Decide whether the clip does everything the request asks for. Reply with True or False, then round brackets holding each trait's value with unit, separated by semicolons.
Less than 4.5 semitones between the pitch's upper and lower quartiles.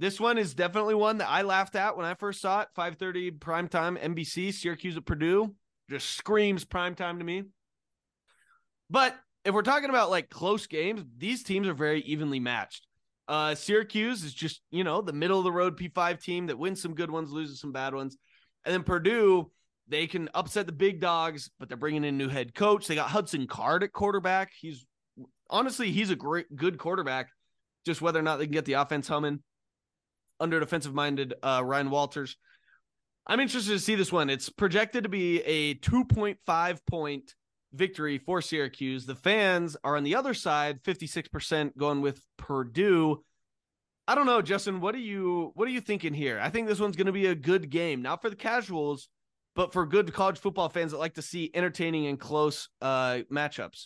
False (4.8 semitones)